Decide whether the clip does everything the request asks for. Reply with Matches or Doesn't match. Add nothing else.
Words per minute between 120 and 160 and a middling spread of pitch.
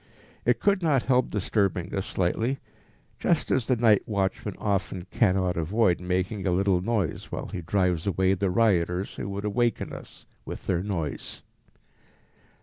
Matches